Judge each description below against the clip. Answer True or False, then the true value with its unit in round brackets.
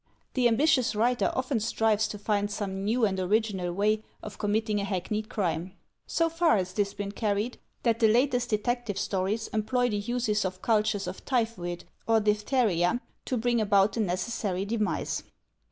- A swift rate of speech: False (165 wpm)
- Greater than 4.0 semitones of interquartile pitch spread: False (2.8 semitones)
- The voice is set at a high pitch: True (215 Hz)